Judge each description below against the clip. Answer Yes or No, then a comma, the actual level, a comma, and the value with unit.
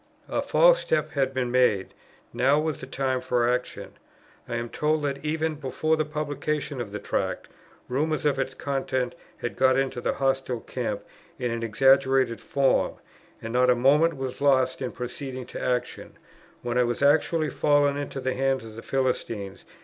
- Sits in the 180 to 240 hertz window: No, low, 135 Hz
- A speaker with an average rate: Yes, average, 175 wpm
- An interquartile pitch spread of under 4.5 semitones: Yes, narrow, 2.6 semitones